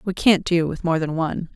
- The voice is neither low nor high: Yes, medium, 170 Hz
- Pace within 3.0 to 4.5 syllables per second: No, 5.6 syllables/s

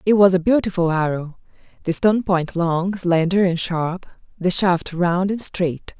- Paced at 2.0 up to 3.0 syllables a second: No, 4.4 syllables/s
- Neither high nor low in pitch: Yes, medium, 180 Hz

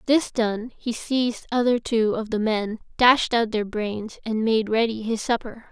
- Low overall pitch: No, high, 225 Hz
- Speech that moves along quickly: No, average, 190 wpm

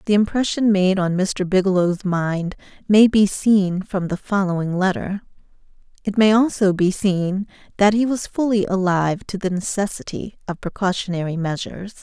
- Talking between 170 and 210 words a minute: No, average, 150 wpm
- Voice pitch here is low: No, high, 195 Hz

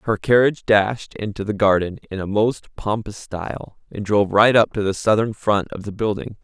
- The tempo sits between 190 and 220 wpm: Yes, fast, 205 wpm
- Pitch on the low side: Yes, low, 105 Hz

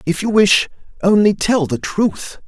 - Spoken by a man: Yes, male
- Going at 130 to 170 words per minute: Yes, average, 145 wpm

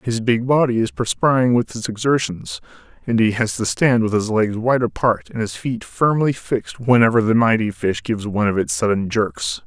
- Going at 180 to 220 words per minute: Yes, fast, 205 wpm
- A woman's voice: No, male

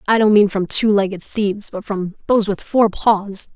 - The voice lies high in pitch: Yes, high, 205 Hz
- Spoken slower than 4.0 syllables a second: No, 4.9 syllables/s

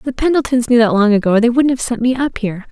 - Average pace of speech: No, fast, 310 wpm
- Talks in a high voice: Yes, high, 240 Hz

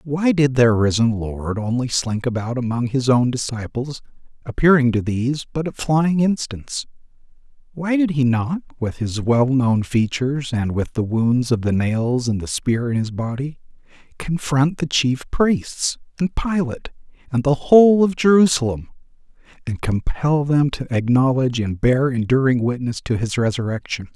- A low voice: Yes, low, 130 Hz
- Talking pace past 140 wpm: Yes, average, 155 wpm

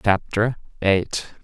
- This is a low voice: Yes, low, 105 Hz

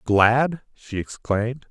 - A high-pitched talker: No, low, 120 Hz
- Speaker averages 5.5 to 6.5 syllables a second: No, 3.4 syllables/s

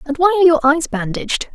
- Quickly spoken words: Yes, fast, 235 wpm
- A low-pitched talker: No, very high, 300 Hz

